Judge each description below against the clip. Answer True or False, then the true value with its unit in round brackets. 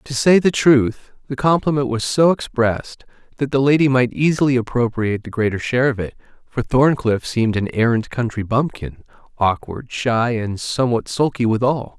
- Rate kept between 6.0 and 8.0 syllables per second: False (5.1 syllables/s)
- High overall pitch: False (125 Hz)